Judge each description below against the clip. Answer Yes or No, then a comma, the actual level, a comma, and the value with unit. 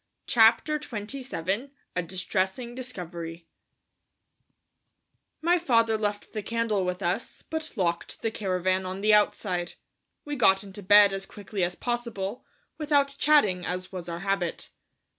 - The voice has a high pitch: Yes, high, 205 Hz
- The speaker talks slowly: Yes, slow, 130 wpm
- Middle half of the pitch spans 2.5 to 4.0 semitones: No, average, 4.5 semitones